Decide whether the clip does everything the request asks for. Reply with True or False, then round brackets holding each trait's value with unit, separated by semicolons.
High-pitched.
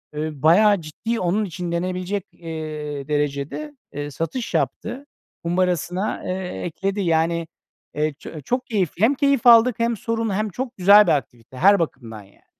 False (180 Hz)